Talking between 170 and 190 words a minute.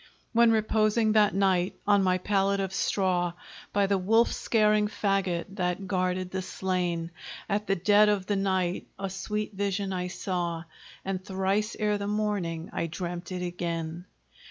No: average, 155 wpm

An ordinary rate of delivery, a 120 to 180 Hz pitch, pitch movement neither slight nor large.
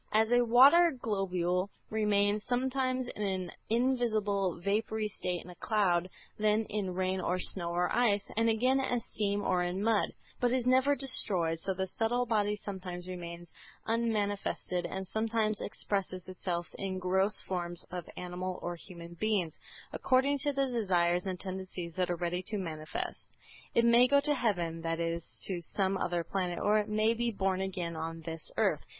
No: average, 170 wpm; high, 195 Hz; average, 4.1 semitones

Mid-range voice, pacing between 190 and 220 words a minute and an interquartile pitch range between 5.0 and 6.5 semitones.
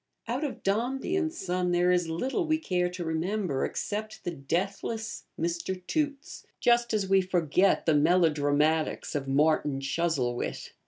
No: medium, 180 Hz; average, 145 wpm; wide, 5.5 semitones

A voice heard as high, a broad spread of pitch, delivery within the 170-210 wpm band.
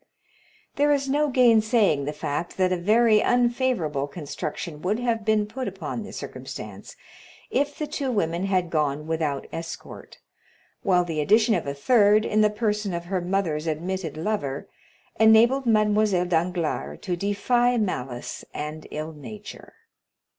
No: high, 195 Hz; wide, 5.7 semitones; average, 145 wpm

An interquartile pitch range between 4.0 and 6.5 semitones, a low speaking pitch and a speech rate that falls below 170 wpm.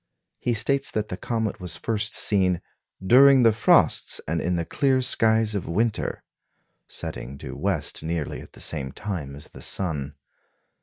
Yes: wide, 5.5 semitones; low, 105 Hz; average, 160 wpm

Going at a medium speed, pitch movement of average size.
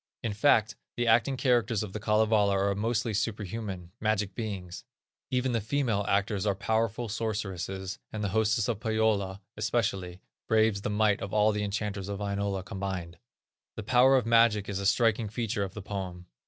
No: average, 170 wpm; narrow, 2.3 semitones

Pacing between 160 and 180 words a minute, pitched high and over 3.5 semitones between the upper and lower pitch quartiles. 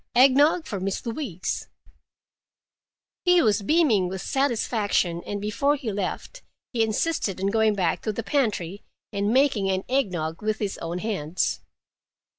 No: average, 150 wpm; high, 215 Hz; wide, 5.6 semitones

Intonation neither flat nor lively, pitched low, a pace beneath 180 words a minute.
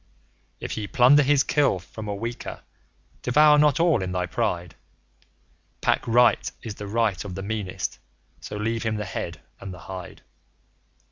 Yes: average, 4.5 semitones; low, 110 Hz; average, 160 wpm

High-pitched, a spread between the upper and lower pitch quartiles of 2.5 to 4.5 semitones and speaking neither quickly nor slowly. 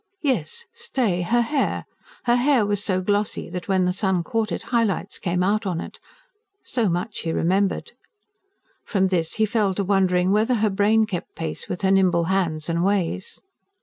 Yes: high, 195 Hz; average, 3.4 semitones; average, 180 wpm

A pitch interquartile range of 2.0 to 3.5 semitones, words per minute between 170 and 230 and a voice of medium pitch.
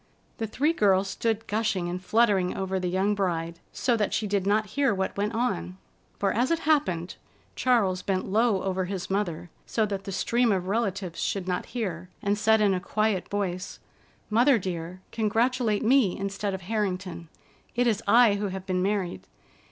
No: average, 3.1 semitones; average, 180 wpm; high, 200 Hz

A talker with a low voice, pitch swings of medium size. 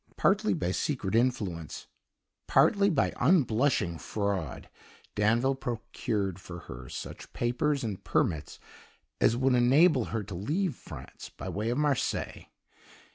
No: low, 120 Hz; wide, 6.2 semitones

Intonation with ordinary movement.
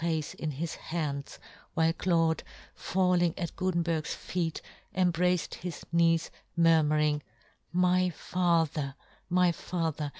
No: narrow, 2.1 semitones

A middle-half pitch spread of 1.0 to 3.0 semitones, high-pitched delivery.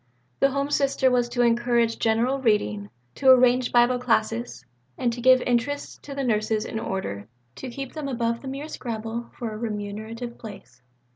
Yes: average, 2.7 semitones; high, 240 Hz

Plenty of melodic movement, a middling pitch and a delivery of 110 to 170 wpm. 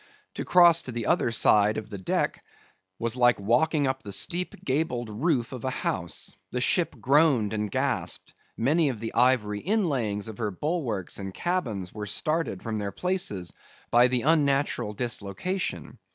No: wide, 6.3 semitones; low, 120 Hz; average, 165 wpm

